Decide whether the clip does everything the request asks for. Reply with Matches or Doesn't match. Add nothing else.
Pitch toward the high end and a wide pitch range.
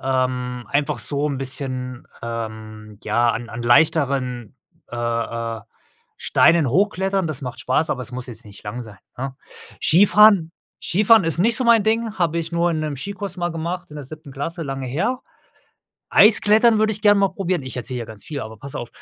Doesn't match